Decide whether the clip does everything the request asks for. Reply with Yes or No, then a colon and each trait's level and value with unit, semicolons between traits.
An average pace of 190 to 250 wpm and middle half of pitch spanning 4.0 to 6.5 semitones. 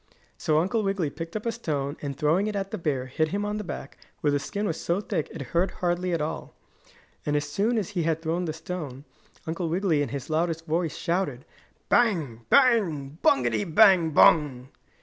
Yes: average, 200 wpm; average, 4.7 semitones